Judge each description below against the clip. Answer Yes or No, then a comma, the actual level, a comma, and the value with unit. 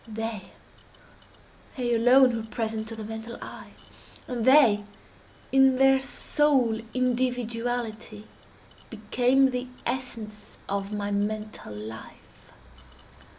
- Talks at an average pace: No, slow, 95 wpm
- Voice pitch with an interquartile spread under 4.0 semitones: Yes, average, 2.8 semitones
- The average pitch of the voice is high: Yes, high, 230 Hz